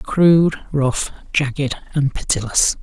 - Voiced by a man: Yes, male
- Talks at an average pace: No, slow, 105 wpm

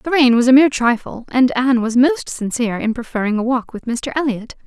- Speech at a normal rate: No, fast, 230 wpm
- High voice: Yes, very high, 250 Hz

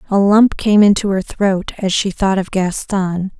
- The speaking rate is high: No, average, 195 wpm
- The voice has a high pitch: Yes, high, 195 Hz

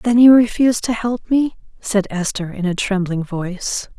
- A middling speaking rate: Yes, average, 180 wpm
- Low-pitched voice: No, high, 210 Hz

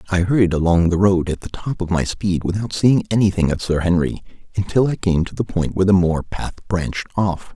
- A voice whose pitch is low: Yes, very low, 90 Hz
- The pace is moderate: No, fast, 230 wpm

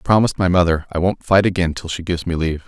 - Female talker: No, male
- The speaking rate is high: Yes, fast, 290 wpm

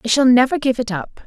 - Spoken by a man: No, female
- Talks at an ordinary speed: No, fast, 285 wpm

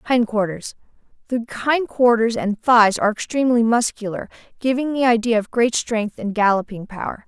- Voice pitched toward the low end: No, high, 210 Hz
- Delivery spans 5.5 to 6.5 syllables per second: No, 5.2 syllables/s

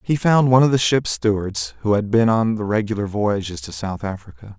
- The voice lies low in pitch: Yes, low, 105 Hz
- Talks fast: Yes, fast, 220 wpm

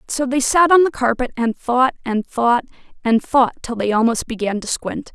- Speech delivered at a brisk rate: Yes, fast, 210 wpm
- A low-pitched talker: No, high, 245 Hz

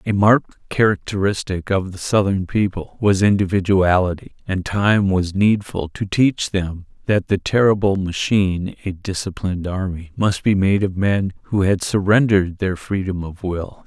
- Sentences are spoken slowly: No, average, 150 wpm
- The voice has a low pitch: Yes, very low, 95 Hz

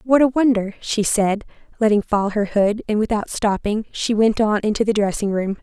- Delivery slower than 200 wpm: No, fast, 205 wpm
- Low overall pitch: No, high, 215 Hz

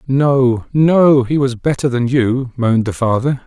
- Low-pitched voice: Yes, low, 130 Hz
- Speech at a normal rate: Yes, average, 175 wpm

